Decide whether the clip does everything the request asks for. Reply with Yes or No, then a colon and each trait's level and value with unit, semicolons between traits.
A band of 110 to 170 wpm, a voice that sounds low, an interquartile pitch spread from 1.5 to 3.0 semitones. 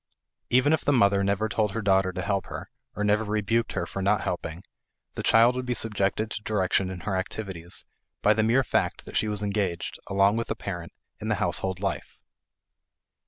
No: average, 200 wpm; low, 100 Hz; narrow, 2.4 semitones